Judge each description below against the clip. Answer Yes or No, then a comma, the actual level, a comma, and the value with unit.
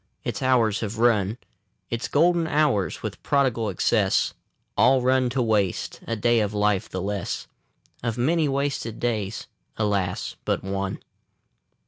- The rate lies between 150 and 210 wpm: No, slow, 135 wpm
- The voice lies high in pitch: No, low, 115 Hz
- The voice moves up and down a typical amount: Yes, average, 4.1 semitones